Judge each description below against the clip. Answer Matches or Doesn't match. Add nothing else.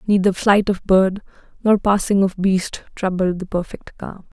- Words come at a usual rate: Matches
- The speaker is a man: Doesn't match